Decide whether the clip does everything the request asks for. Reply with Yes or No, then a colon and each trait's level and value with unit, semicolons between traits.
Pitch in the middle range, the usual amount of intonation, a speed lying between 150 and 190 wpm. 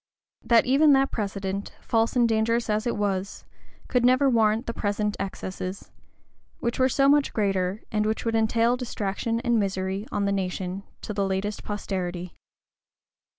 No: high, 215 Hz; average, 3.2 semitones; average, 155 wpm